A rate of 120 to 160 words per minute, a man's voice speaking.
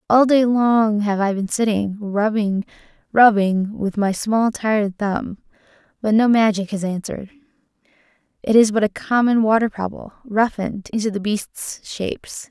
No: average, 150 wpm; female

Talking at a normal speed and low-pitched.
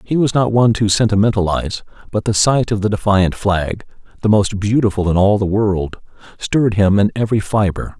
Yes: average, 190 wpm; low, 105 Hz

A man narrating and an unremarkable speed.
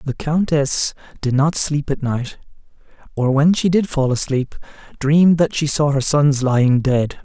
Yes: male; average, 175 wpm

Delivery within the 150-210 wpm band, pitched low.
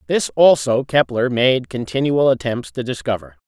No: average, 140 wpm; low, 125 Hz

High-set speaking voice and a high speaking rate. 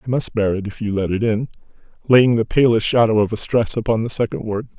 No: low, 110 Hz; fast, 250 wpm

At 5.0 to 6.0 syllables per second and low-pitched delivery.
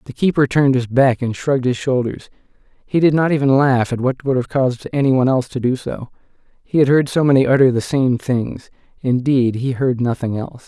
Yes: 5.8 syllables/s; low, 130 Hz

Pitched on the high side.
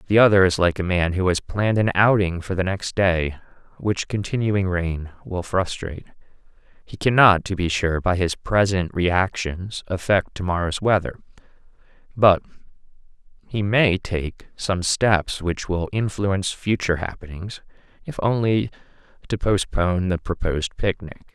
No: very low, 95 Hz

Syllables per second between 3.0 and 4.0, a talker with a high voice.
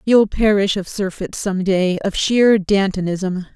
Yes: 3.9 syllables/s; high, 195 Hz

